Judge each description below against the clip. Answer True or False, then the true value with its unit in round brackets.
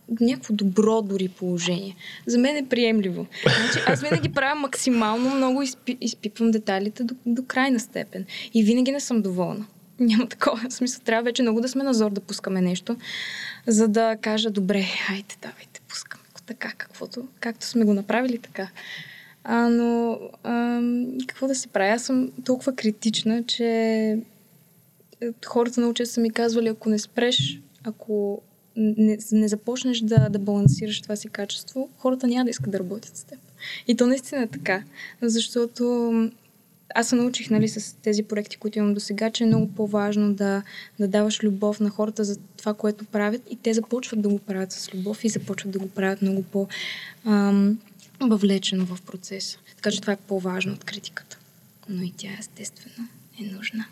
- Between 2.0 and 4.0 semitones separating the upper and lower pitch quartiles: True (3.0 semitones)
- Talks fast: True (170 wpm)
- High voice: True (215 Hz)